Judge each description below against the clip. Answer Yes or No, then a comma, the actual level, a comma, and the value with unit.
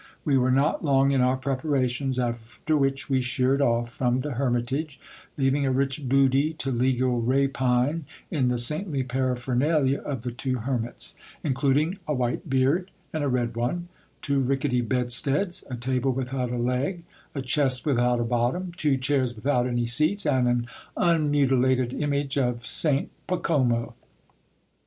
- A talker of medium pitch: No, low, 130 Hz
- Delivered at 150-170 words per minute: Yes, average, 155 wpm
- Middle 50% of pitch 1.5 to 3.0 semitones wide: Yes, narrow, 2.4 semitones